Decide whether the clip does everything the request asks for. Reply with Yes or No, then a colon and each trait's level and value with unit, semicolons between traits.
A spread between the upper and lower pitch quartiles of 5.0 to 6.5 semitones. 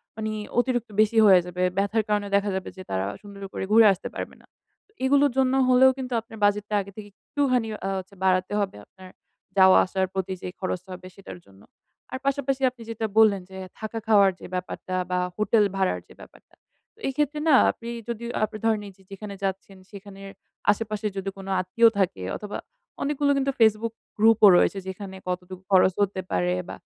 No: average, 3.3 semitones